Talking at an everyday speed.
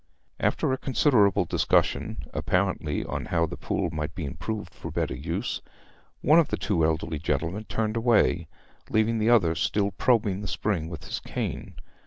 Yes: average, 165 wpm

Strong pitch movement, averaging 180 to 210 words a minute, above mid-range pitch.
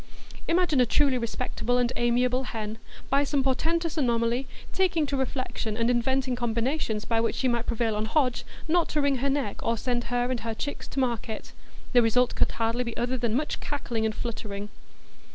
No: average, 2.9 semitones; average, 190 wpm; high, 245 Hz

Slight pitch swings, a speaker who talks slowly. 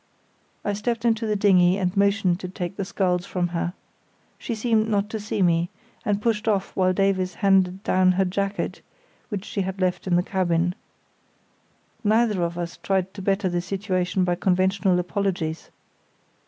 No: narrow, 2.3 semitones; average, 170 wpm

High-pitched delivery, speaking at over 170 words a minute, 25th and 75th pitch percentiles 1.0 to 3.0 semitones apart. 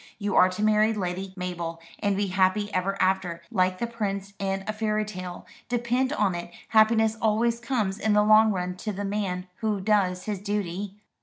Yes: high, 205 Hz; average, 185 wpm; narrow, 2.6 semitones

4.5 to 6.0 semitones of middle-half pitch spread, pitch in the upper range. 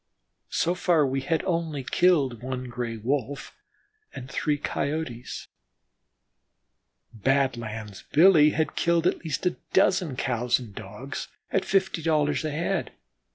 No: average, 4.9 semitones; medium, 145 Hz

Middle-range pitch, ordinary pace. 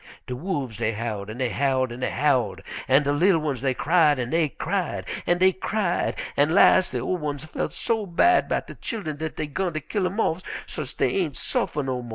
No: medium, 150 Hz; fast, 225 wpm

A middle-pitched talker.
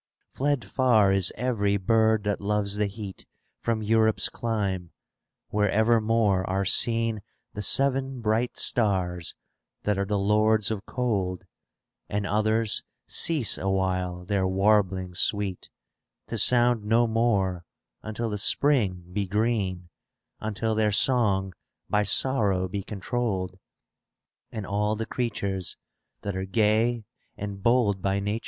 No: low, 105 Hz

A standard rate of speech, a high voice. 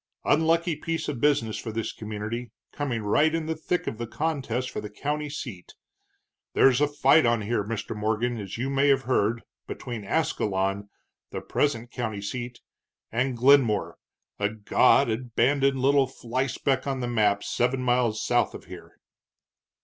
No: average, 155 wpm; low, 125 Hz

